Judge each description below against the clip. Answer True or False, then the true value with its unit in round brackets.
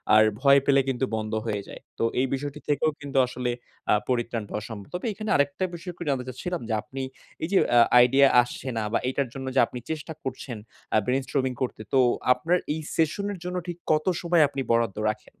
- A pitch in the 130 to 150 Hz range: True (135 Hz)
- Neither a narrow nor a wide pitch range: True (4.4 semitones)